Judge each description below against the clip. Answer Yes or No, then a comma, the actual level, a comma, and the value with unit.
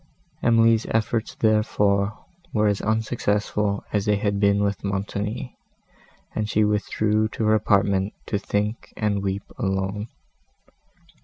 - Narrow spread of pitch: Yes, narrow, 1.4 semitones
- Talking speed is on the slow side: Yes, slow, 125 wpm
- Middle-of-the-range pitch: No, low, 105 Hz